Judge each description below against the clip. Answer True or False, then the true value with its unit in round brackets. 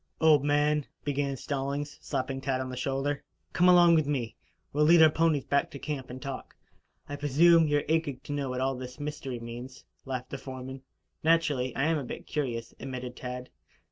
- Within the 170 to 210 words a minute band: True (195 wpm)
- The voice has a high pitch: False (140 Hz)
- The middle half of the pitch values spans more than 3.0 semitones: False (2.5 semitones)